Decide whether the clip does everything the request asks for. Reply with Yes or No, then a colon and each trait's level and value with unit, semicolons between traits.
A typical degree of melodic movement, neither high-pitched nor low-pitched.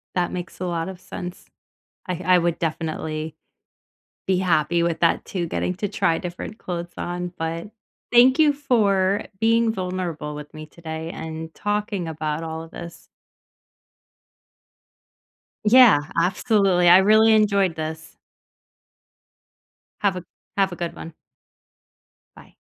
Yes: average, 3.5 semitones; medium, 175 Hz